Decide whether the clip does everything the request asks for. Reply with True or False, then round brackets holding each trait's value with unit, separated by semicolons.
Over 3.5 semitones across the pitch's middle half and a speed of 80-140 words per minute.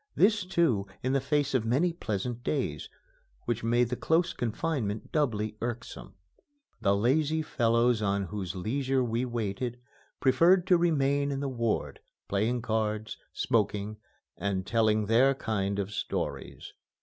True (4.5 semitones; 135 wpm)